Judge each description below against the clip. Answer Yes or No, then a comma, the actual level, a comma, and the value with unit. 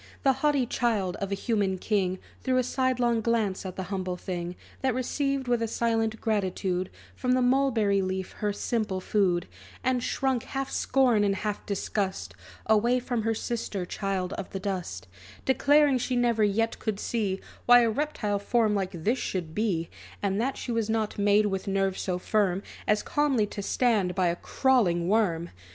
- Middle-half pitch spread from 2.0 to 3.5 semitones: No, average, 4.2 semitones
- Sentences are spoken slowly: No, average, 175 wpm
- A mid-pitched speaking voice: No, high, 210 Hz